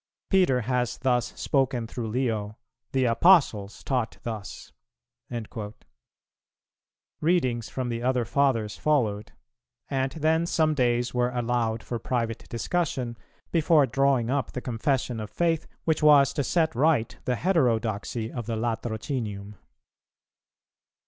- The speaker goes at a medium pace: No, slow, 120 wpm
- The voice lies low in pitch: Yes, low, 125 Hz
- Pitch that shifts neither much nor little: Yes, average, 3.5 semitones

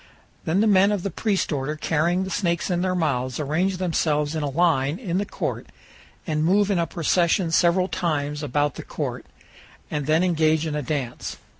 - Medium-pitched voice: Yes, medium, 165 Hz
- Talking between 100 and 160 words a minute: No, average, 190 wpm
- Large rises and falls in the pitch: No, average, 3.6 semitones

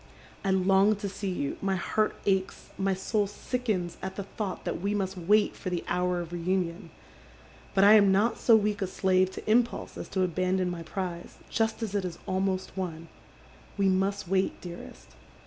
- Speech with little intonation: Yes, narrow, 1.9 semitones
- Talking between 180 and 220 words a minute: Yes, average, 190 wpm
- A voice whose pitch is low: No, high, 190 Hz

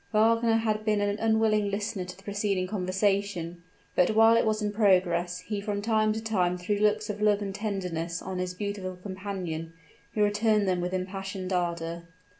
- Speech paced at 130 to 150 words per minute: No, average, 180 wpm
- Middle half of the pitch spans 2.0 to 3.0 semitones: Yes, average, 2.7 semitones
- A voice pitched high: Yes, high, 200 Hz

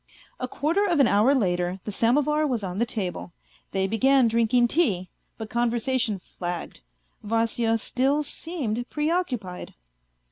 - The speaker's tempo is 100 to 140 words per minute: Yes, slow, 135 wpm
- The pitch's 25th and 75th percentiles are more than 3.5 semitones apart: Yes, average, 5.1 semitones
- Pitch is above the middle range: Yes, high, 235 Hz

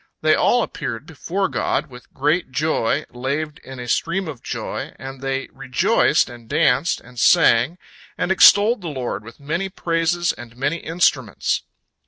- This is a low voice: No, medium, 145 Hz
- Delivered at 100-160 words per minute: Yes, average, 155 wpm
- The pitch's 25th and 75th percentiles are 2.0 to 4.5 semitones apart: No, average, 5.1 semitones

